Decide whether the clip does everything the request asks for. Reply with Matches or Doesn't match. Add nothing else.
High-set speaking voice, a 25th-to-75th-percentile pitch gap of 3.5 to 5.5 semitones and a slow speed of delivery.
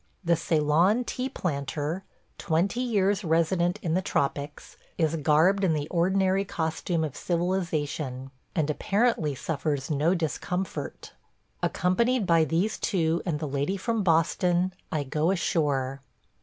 Doesn't match